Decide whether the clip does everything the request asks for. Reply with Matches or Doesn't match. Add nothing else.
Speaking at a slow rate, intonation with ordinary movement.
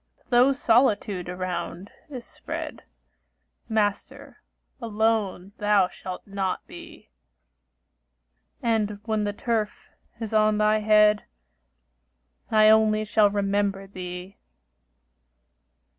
Doesn't match